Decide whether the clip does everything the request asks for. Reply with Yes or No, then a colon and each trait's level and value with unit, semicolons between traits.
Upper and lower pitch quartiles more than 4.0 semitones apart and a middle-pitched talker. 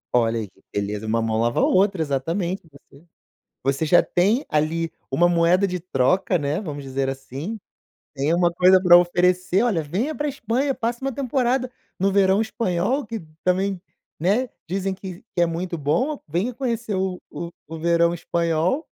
Yes: average, 4.6 semitones; medium, 180 Hz